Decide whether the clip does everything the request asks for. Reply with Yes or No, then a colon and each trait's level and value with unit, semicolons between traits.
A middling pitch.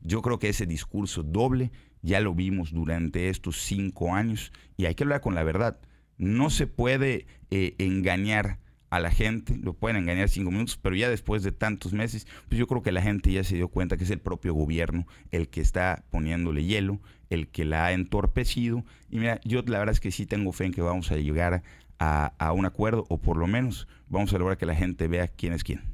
No: very low, 95 Hz